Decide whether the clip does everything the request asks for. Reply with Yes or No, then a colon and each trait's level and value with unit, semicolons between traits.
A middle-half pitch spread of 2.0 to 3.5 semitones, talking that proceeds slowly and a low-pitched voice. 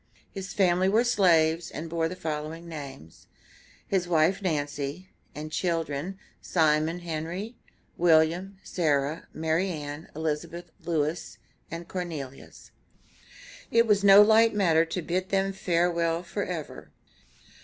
No: average, 3.0 semitones; slow, 115 wpm; medium, 170 Hz